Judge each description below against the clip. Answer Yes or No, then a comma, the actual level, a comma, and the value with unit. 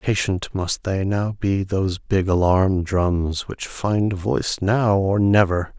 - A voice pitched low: Yes, very low, 95 Hz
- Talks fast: No, average, 165 wpm